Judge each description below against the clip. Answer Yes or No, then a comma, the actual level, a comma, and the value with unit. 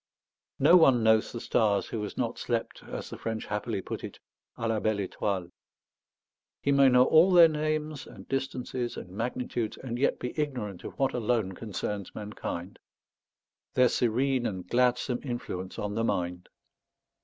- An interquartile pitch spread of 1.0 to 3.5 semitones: No, average, 4.2 semitones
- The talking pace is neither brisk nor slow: Yes, average, 160 wpm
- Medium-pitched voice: No, low, 120 Hz